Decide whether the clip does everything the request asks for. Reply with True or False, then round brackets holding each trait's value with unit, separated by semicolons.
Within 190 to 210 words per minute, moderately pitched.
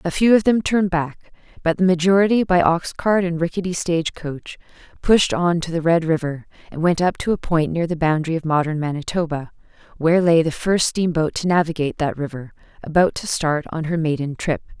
True (200 wpm; 170 Hz)